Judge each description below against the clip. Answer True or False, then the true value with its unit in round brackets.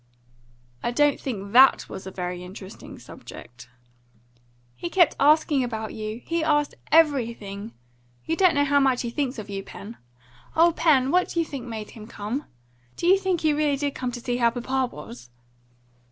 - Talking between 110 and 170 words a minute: False (180 wpm)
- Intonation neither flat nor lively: False (5.7 semitones)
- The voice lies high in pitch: True (255 Hz)